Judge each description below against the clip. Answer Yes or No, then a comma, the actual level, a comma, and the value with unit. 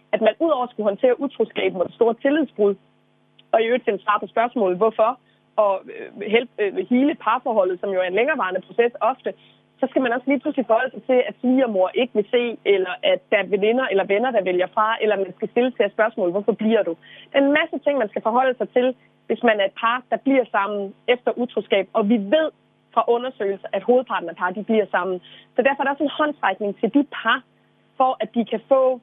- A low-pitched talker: No, high, 225 Hz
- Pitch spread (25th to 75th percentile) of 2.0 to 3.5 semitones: No, average, 3.9 semitones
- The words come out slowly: No, fast, 225 wpm